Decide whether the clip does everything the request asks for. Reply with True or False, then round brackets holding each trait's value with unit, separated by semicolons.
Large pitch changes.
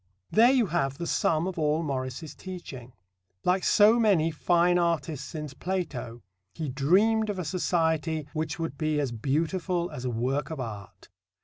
False (4.6 semitones)